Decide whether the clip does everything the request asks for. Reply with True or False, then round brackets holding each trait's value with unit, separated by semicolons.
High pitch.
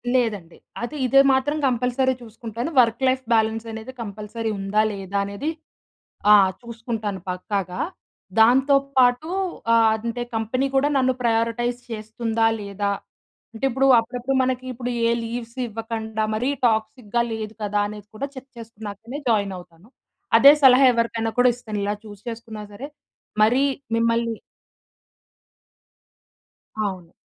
True (230 Hz)